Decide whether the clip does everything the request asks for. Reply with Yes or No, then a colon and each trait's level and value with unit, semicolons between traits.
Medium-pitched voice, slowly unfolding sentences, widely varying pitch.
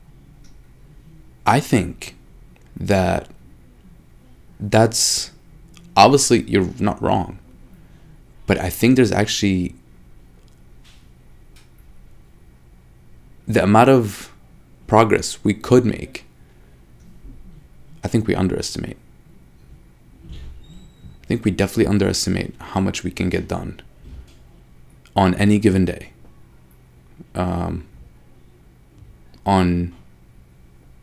No: very low, 85 Hz; slow, 80 wpm; wide, 8.4 semitones